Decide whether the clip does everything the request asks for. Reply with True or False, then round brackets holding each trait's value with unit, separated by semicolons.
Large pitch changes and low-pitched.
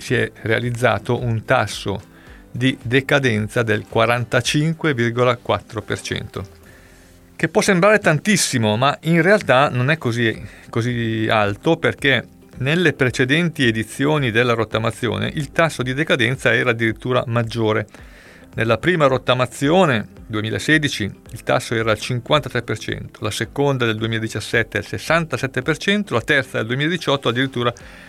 False (4.3 semitones; 120 Hz)